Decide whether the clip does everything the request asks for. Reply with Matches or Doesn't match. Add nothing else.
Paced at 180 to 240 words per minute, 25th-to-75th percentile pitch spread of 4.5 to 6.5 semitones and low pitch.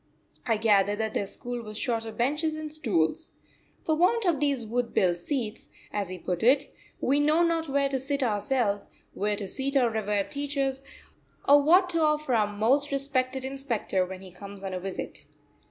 Doesn't match